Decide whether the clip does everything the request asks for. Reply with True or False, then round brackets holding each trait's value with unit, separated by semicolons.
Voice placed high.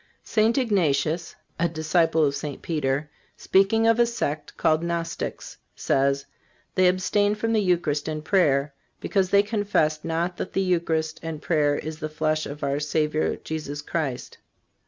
False (160 Hz)